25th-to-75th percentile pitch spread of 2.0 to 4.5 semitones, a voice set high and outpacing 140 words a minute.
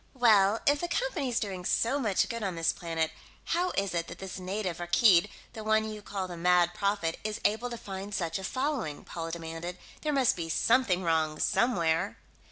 No: average, 5.0 semitones; high, 195 Hz; average, 190 wpm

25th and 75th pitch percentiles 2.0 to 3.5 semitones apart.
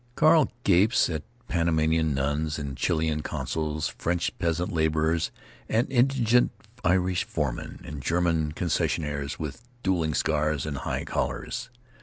Yes: average, 2.8 semitones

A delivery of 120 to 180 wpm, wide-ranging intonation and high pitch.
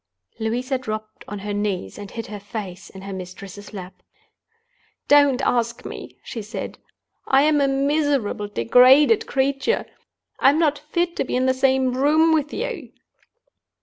Yes: average, 150 wpm; wide, 5.7 semitones; very high, 255 Hz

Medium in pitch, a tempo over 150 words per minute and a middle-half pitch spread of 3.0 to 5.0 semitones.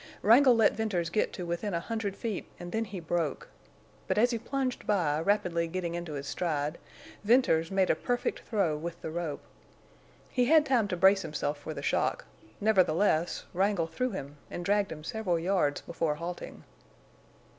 Yes: medium, 180 Hz; average, 175 wpm; average, 4.5 semitones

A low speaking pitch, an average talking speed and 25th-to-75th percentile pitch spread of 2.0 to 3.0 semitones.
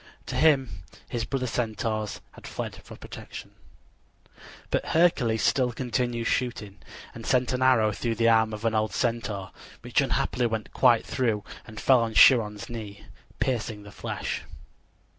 Yes: low, 115 Hz; average, 150 wpm; narrow, 2.6 semitones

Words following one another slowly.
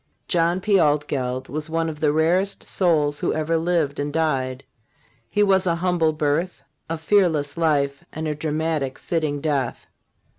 No: average, 155 wpm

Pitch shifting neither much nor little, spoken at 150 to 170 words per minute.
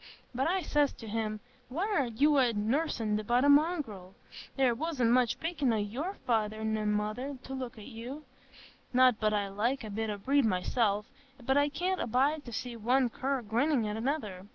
No: average, 4.6 semitones; average, 190 wpm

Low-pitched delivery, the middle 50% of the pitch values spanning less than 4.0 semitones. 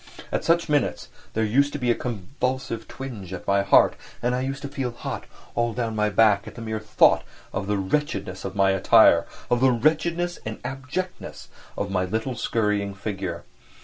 No: low, 115 Hz; average, 5.0 semitones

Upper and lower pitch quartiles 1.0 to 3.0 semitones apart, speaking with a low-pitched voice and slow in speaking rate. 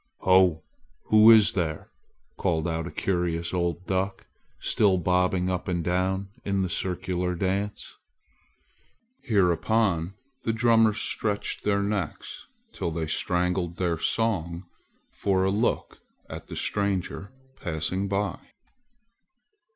Yes: narrow, 2.4 semitones; very low, 95 Hz; slow, 115 wpm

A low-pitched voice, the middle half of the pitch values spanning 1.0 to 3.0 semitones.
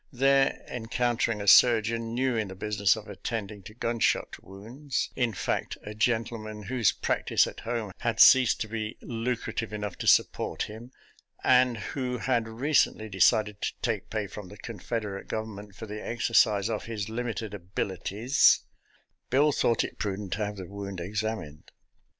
Yes: low, 110 Hz; narrow, 2.6 semitones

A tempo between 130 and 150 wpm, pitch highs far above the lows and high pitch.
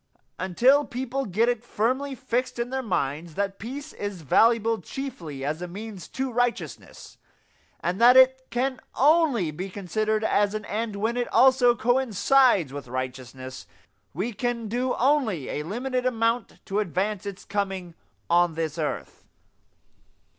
Yes: average, 145 wpm; wide, 5.7 semitones; high, 220 Hz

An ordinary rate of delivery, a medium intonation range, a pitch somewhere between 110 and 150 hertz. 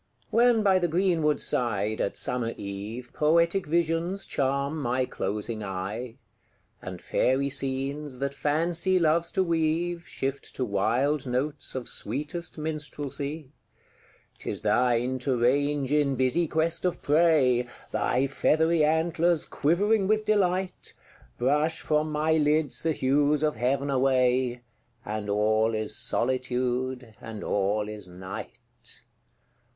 No: slow, 125 wpm; average, 4.6 semitones; medium, 140 Hz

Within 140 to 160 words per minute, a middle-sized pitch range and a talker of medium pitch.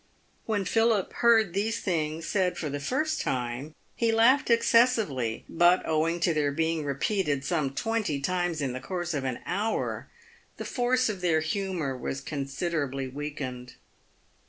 No: average, 150 wpm; wide, 7.0 semitones; medium, 165 Hz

